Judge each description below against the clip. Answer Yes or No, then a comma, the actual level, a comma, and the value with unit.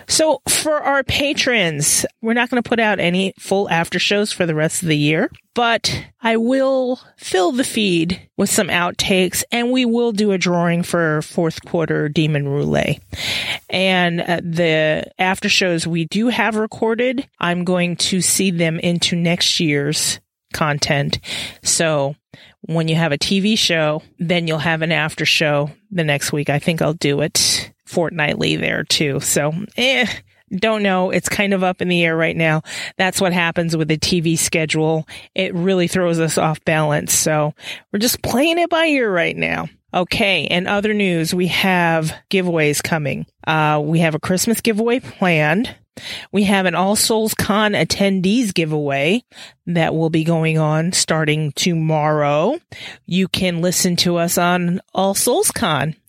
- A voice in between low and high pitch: Yes, medium, 175 Hz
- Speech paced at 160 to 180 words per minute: Yes, average, 165 wpm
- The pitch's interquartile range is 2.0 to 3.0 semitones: No, average, 4.4 semitones